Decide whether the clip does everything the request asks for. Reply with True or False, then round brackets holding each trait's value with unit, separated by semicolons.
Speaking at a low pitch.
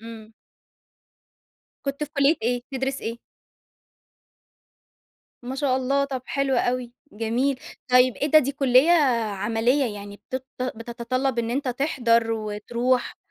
False (250 Hz)